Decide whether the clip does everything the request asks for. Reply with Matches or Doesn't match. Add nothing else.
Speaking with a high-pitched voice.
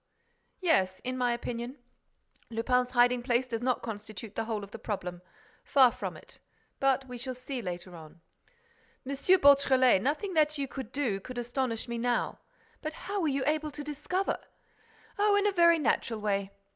Matches